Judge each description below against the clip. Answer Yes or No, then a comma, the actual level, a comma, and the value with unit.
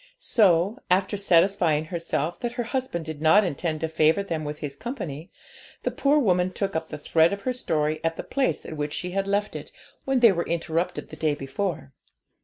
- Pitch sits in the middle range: Yes, medium, 170 Hz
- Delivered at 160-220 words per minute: Yes, fast, 205 wpm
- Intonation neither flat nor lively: Yes, average, 4.3 semitones